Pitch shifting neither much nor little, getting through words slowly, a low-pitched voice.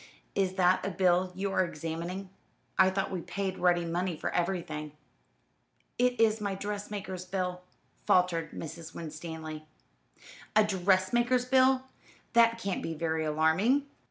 No: average, 3.2 semitones; slow, 130 wpm; medium, 185 Hz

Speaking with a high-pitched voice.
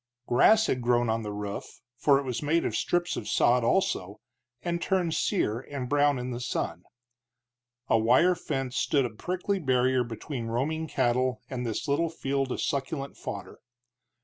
No: low, 130 Hz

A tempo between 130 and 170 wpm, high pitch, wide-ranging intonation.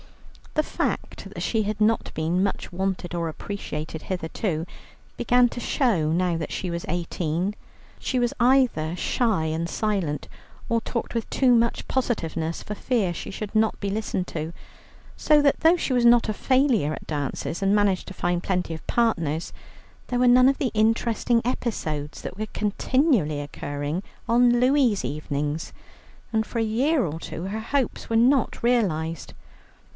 Yes: average, 160 wpm; high, 205 Hz; wide, 6.4 semitones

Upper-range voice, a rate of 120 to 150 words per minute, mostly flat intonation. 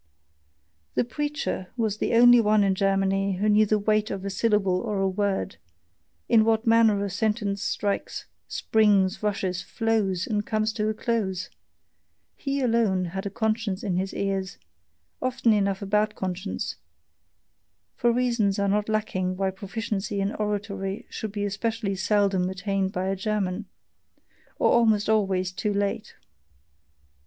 Yes: high, 205 Hz; average, 145 wpm; narrow, 2.2 semitones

